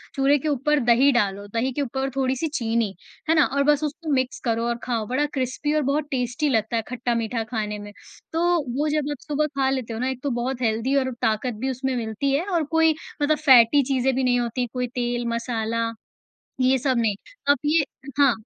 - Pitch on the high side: Yes, very high, 255 Hz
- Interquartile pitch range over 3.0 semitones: Yes, average, 3.4 semitones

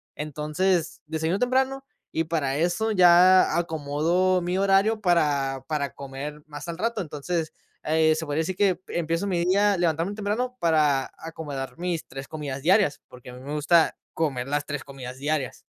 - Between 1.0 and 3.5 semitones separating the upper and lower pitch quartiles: No, average, 3.9 semitones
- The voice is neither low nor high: Yes, medium, 160 Hz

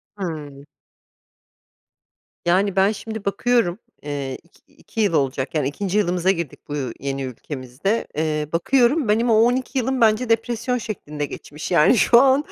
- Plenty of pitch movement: Yes, wide, 7.4 semitones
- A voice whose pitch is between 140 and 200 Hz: Yes, high, 190 Hz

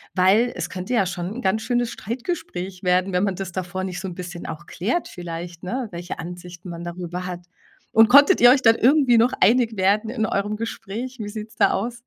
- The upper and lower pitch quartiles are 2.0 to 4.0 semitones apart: No, average, 4.4 semitones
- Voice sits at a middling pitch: No, high, 195 Hz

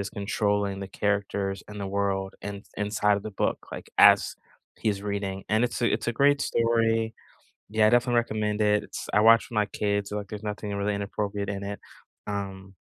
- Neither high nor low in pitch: No, low, 105 Hz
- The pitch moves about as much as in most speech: No, narrow, 1.3 semitones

